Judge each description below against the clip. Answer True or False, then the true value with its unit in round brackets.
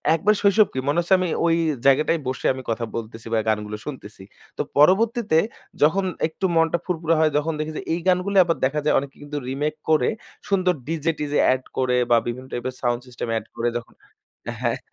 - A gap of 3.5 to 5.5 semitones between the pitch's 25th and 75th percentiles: True (4.8 semitones)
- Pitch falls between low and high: True (150 Hz)